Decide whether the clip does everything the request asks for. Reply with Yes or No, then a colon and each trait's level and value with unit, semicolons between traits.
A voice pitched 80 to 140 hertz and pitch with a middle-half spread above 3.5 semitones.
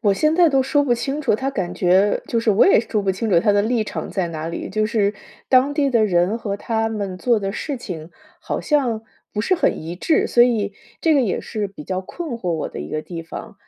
No: high, 215 Hz; average, 5.1 semitones